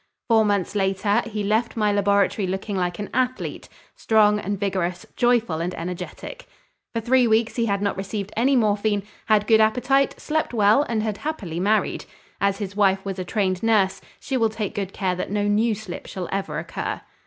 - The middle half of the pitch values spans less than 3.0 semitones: Yes, narrow, 2.5 semitones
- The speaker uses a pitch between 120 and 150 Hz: No, high, 205 Hz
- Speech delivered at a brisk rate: No, average, 190 wpm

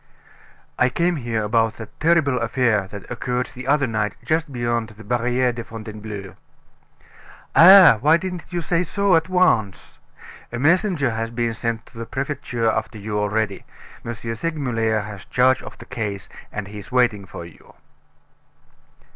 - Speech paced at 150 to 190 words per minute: Yes, average, 155 wpm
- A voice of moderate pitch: No, low, 120 Hz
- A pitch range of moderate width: Yes, average, 4.4 semitones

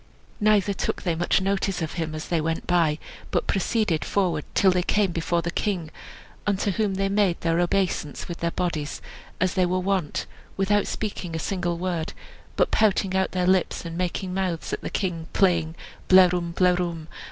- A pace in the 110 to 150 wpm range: No, average, 180 wpm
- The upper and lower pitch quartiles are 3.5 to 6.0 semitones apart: No, narrow, 2.5 semitones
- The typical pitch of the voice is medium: Yes, medium, 180 Hz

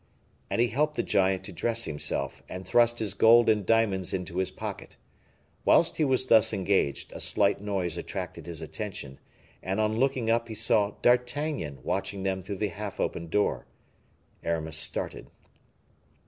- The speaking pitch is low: Yes, low, 100 Hz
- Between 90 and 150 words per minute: No, average, 160 wpm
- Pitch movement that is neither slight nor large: Yes, average, 3.9 semitones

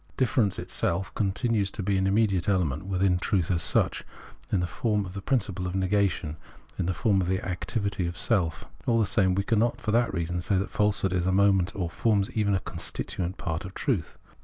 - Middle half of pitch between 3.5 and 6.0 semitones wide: No, narrow, 2.4 semitones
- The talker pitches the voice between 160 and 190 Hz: No, very low, 95 Hz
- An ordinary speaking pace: No, fast, 210 wpm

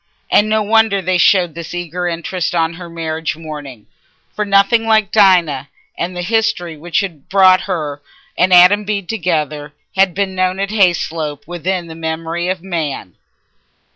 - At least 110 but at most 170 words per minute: Yes, average, 160 wpm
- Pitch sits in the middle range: Yes, medium, 175 Hz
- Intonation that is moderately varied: Yes, average, 3.2 semitones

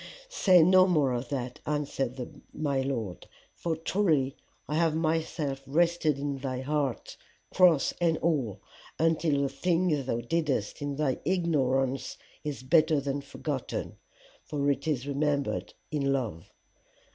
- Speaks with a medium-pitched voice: Yes, medium, 145 Hz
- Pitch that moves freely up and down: No, average, 3.2 semitones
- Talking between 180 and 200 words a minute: No, slow, 135 wpm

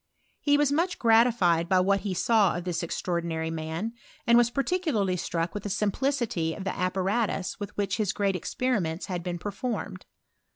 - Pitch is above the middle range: Yes, high, 195 Hz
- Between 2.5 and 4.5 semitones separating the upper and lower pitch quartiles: No, average, 5.0 semitones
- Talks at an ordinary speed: Yes, average, 180 wpm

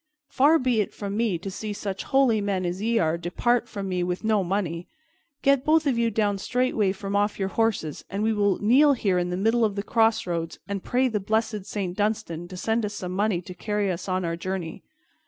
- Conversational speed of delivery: No, fast, 225 wpm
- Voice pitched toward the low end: No, high, 205 Hz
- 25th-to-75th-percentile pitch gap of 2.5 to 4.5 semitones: Yes, average, 3.4 semitones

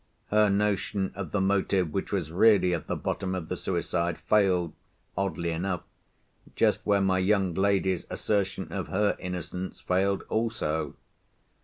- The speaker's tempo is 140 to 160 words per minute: Yes, average, 145 wpm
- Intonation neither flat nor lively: No, narrow, 2.1 semitones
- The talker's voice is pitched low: Yes, very low, 95 Hz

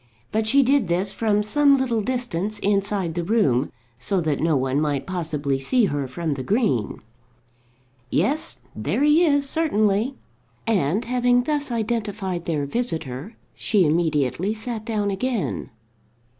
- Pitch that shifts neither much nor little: No, wide, 7.3 semitones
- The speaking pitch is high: Yes, high, 205 Hz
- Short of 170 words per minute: Yes, average, 140 wpm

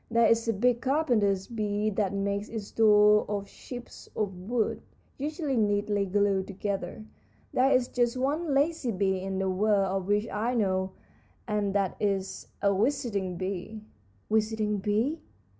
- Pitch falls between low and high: No, high, 210 Hz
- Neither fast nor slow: Yes, average, 150 wpm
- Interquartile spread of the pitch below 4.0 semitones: Yes, average, 3.1 semitones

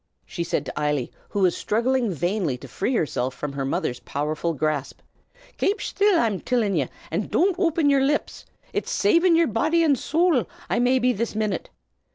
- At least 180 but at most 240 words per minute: Yes, average, 185 wpm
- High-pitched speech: Yes, high, 225 Hz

